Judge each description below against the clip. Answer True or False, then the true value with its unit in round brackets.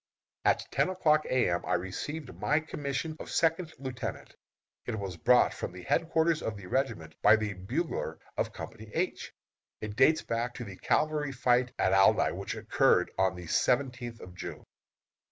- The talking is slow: False (170 wpm)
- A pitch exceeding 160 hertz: False (120 Hz)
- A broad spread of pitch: True (7.4 semitones)